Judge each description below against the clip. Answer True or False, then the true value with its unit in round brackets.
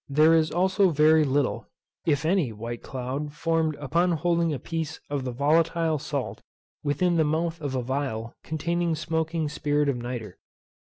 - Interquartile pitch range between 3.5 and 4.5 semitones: False (3.1 semitones)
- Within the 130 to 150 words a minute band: False (160 wpm)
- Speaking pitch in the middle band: True (155 Hz)